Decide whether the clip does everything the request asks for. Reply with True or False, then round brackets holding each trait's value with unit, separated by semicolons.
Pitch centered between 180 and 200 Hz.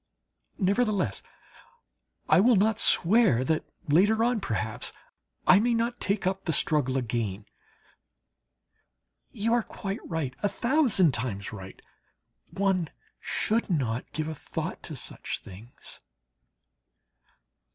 True (185 Hz)